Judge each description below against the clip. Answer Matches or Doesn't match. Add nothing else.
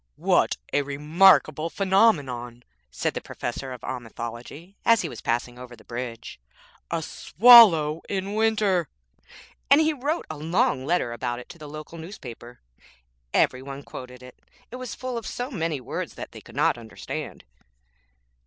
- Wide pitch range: Matches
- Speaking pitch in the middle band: Matches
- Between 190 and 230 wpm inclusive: Doesn't match